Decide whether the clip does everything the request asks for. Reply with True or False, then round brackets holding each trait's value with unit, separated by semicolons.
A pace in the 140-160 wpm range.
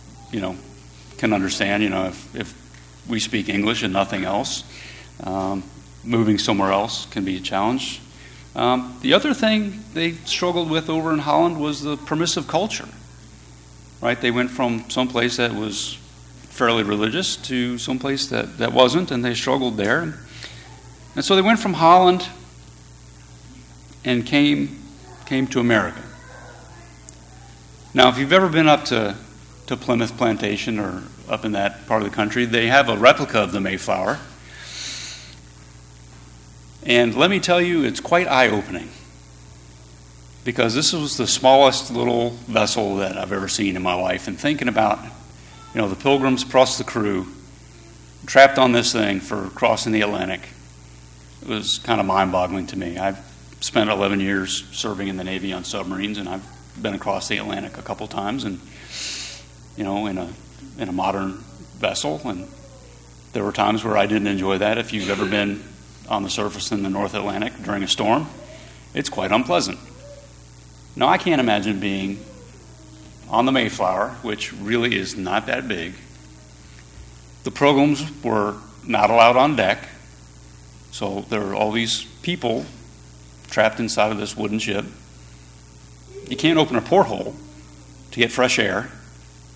True (155 wpm)